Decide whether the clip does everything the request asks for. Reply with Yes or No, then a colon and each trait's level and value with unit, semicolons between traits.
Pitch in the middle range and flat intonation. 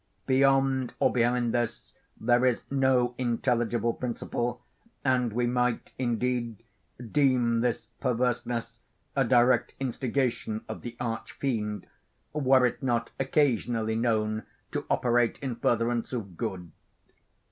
No: low, 120 Hz; narrow, 1.8 semitones